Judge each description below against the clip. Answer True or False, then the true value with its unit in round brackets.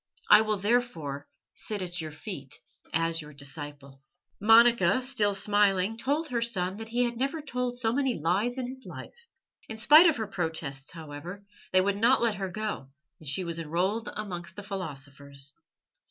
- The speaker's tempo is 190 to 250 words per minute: False (170 wpm)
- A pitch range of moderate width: False (6.4 semitones)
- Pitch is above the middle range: True (200 Hz)